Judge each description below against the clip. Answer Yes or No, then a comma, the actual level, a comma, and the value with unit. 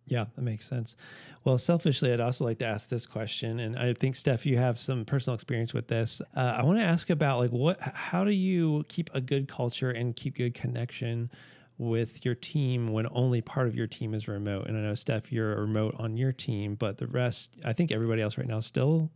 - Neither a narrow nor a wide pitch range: Yes, average, 3.3 semitones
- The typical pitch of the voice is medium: No, low, 125 Hz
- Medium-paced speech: No, fast, 230 wpm